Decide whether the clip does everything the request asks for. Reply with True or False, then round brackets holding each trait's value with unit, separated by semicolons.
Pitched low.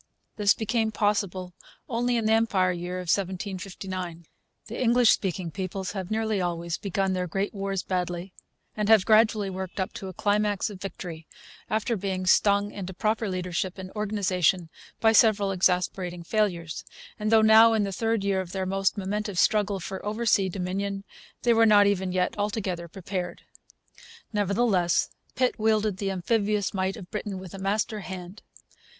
False (195 Hz)